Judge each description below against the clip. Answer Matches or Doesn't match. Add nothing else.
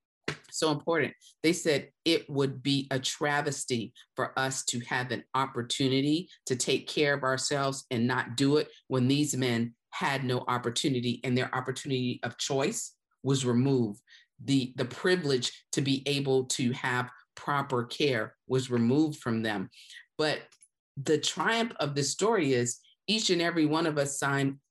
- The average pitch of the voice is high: Doesn't match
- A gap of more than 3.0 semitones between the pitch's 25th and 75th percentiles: Doesn't match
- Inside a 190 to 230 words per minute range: Doesn't match